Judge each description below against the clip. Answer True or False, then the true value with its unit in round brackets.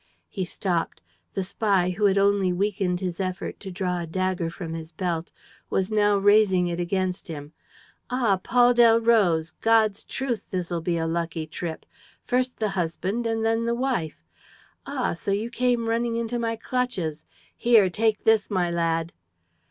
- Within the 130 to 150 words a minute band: False (160 wpm)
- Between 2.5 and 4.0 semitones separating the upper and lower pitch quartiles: False (4.5 semitones)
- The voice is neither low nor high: False (195 Hz)